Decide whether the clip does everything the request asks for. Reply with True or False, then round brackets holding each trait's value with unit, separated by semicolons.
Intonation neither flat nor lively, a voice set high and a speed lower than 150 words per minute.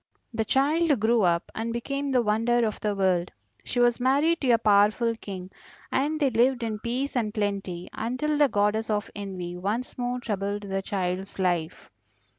False (3.9 semitones; 220 Hz; 175 wpm)